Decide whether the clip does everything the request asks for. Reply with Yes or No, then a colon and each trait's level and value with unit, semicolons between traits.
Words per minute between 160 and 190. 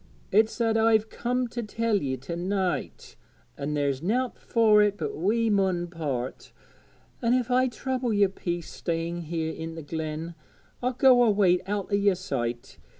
Yes: average, 165 wpm